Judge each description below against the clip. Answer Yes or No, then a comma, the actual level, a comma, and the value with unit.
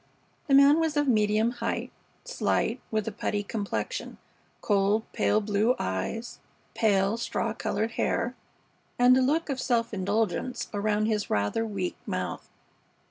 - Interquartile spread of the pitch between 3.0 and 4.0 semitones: Yes, average, 3.4 semitones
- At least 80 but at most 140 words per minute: Yes, slow, 135 wpm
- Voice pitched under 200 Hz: No, high, 220 Hz